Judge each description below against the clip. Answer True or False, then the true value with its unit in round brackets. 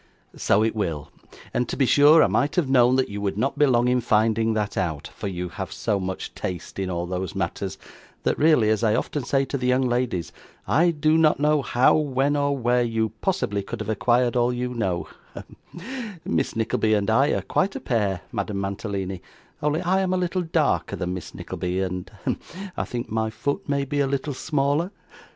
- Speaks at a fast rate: True (210 wpm)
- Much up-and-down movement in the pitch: True (6.0 semitones)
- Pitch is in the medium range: False (120 Hz)